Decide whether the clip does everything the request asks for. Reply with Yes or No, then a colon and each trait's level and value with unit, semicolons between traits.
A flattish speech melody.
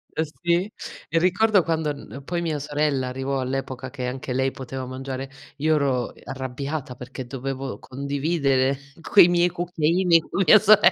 No: average, 4.2 semitones